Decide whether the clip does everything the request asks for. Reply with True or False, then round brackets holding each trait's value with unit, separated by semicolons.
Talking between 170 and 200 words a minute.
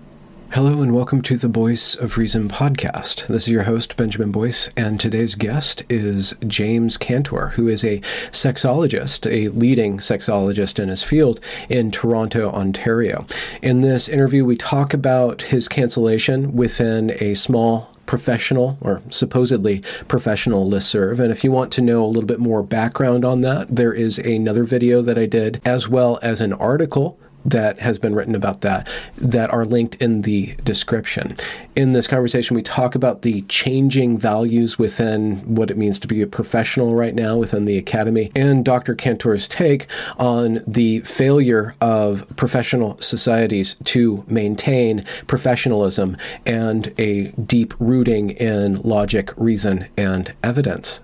False (155 wpm)